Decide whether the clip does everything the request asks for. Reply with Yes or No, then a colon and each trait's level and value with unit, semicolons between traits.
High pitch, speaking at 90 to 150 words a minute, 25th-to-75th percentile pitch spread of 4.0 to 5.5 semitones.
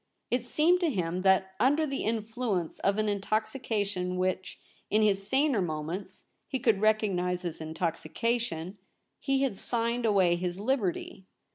Yes: high, 205 Hz; average, 140 wpm; average, 4.5 semitones